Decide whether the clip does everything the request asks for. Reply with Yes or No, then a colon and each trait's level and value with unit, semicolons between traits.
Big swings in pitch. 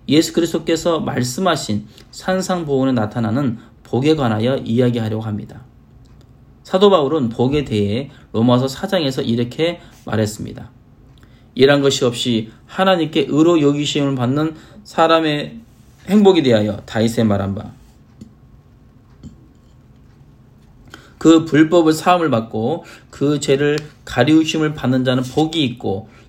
No: average, 5.0 semitones